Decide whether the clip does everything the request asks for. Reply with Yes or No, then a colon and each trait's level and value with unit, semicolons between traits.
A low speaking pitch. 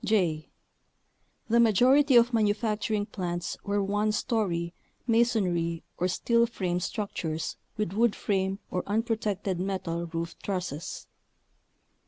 No: high, 200 Hz